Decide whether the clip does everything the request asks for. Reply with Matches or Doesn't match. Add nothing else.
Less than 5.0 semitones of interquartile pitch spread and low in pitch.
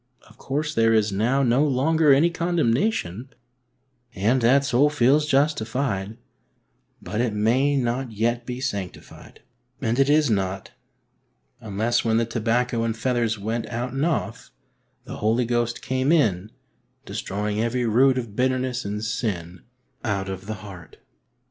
Matches